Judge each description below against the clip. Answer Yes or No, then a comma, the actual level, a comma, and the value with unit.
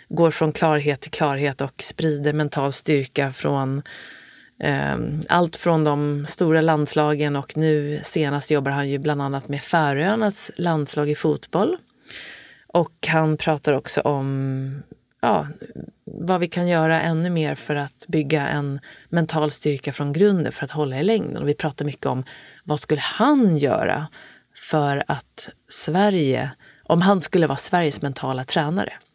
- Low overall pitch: No, medium, 150 Hz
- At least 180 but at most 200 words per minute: No, average, 150 wpm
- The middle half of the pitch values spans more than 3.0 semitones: No, average, 2.7 semitones